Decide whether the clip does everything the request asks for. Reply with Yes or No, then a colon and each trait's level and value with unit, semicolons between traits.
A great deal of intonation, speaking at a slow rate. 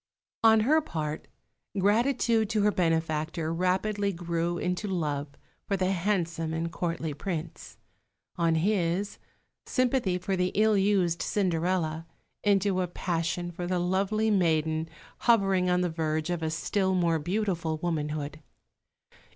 No: average, 3.5 semitones; slow, 130 wpm